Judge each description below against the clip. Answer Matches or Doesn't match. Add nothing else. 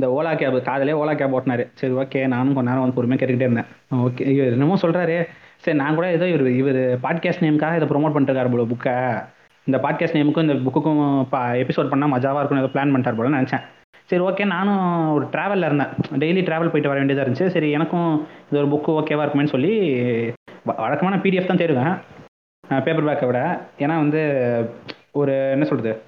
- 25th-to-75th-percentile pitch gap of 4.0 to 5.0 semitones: Doesn't match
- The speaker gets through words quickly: Matches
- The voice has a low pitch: Doesn't match